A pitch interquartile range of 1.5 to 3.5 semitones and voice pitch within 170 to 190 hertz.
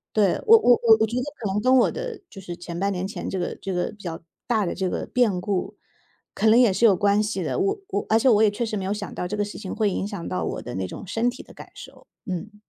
No: average, 3.2 semitones; high, 205 Hz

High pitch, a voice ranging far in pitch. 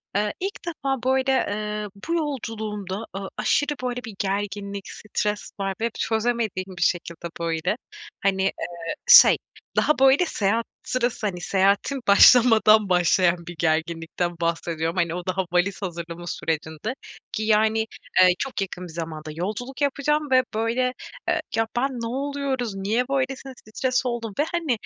Yes: high, 210 Hz; wide, 5.9 semitones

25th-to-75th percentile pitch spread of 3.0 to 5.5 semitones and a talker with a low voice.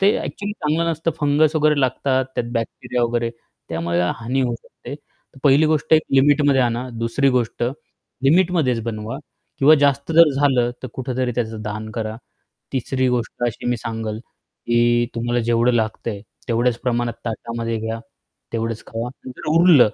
Yes: average, 3.5 semitones; low, 125 Hz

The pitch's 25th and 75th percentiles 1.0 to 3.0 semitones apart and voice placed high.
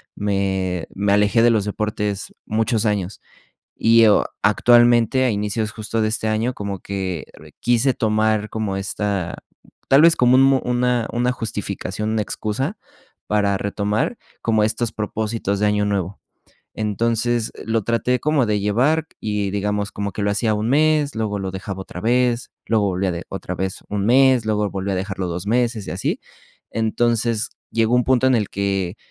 No: average, 2.7 semitones; low, 110 Hz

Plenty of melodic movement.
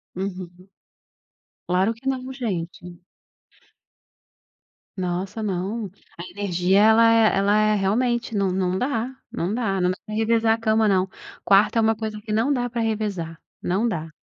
No: average, 3.5 semitones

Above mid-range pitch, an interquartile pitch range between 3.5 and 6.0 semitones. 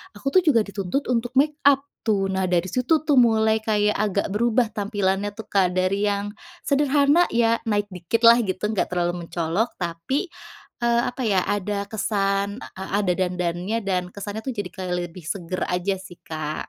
Yes: high, 205 Hz; average, 4.0 semitones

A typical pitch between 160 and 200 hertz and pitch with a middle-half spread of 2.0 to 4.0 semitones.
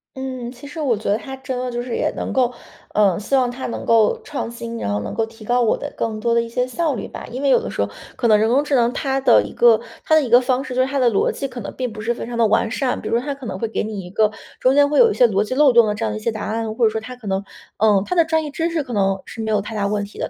No: high, 240 Hz; average, 3.5 semitones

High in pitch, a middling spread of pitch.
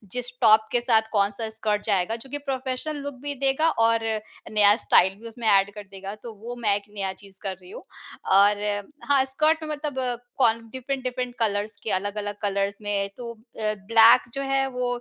Yes: high, 225 Hz; average, 3.8 semitones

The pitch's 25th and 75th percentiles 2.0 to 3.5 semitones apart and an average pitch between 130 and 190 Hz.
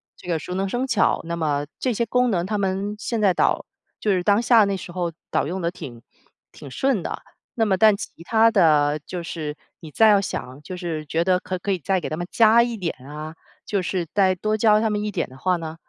No: average, 4.2 semitones; medium, 185 Hz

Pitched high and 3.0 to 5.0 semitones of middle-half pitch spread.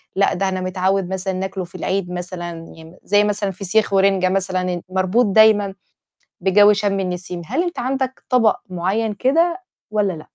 No: high, 195 Hz; narrow, 2.4 semitones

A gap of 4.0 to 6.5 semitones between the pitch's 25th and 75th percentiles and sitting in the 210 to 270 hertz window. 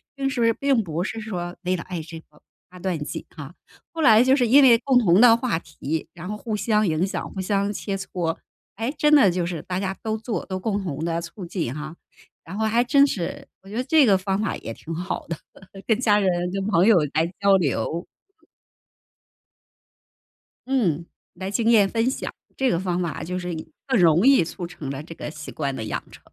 No: average, 5.0 semitones; high, 190 Hz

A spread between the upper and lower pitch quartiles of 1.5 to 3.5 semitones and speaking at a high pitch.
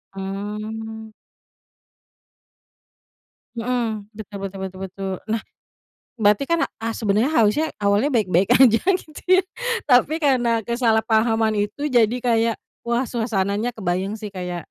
Yes: average, 3.0 semitones; high, 220 Hz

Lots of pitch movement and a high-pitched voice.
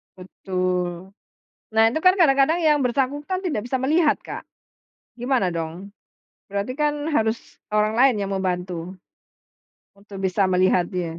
Yes: wide, 6.7 semitones; high, 205 Hz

